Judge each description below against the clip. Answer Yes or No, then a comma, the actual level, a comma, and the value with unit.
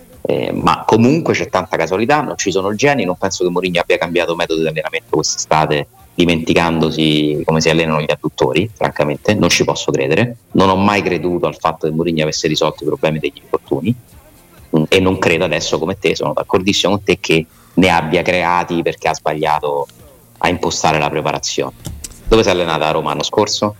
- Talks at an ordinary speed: No, fast, 185 wpm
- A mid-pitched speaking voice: No, very low, 85 Hz